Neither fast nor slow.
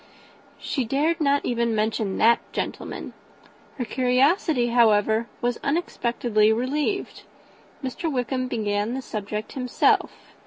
No: slow, 110 wpm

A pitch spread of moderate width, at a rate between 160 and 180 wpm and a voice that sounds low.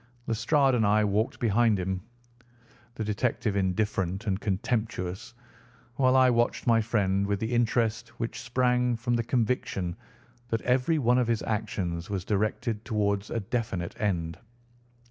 No: average, 3.4 semitones; average, 145 wpm; low, 110 Hz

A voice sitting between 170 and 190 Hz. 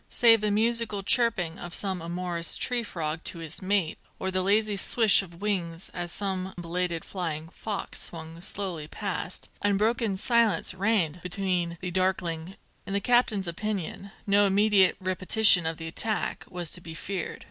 Yes: medium, 185 Hz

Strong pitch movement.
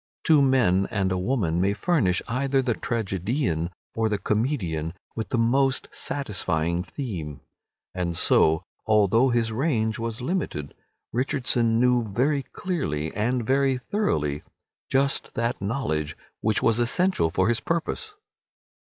Yes: wide, 6.3 semitones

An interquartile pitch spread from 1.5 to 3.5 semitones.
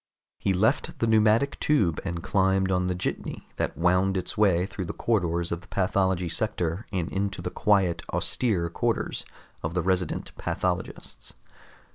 Yes: average, 2.7 semitones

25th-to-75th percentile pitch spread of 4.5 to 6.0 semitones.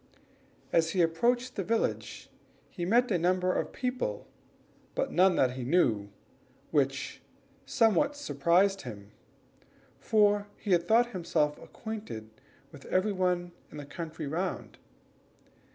Yes: average, 5.2 semitones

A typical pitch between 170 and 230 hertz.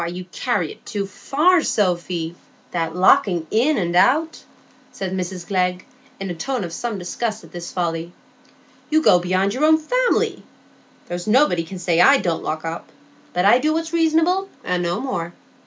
Yes: high, 190 Hz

